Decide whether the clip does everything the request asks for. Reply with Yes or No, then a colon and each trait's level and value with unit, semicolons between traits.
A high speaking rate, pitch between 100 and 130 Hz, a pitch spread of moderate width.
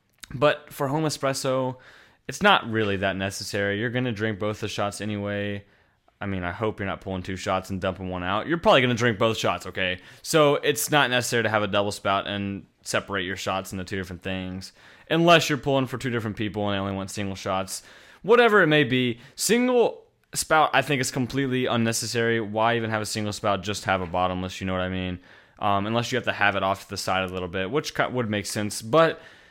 Yes: fast, 230 wpm; low, 105 Hz; average, 4.7 semitones